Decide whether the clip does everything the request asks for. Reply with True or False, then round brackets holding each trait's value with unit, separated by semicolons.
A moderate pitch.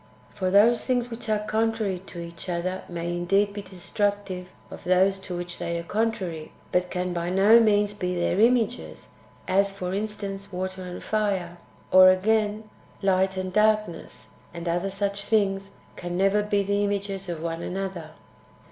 False (195 Hz)